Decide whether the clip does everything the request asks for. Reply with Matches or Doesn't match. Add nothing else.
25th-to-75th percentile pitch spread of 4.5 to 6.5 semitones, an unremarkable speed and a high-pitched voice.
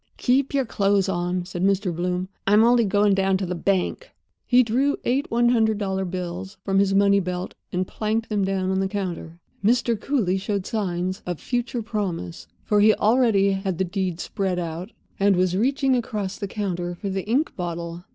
Doesn't match